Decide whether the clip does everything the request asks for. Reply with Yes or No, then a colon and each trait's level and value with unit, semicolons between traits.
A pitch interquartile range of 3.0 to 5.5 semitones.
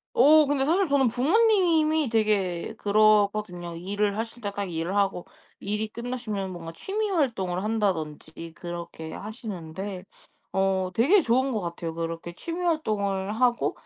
No: wide, 6.1 semitones